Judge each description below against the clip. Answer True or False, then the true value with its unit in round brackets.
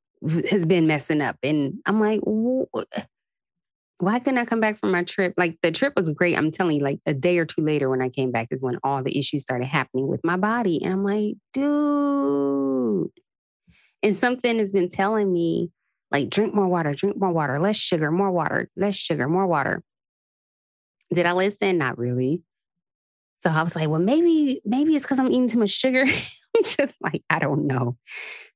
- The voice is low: False (180 Hz)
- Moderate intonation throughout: False (6.0 semitones)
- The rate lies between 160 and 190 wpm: False (200 wpm)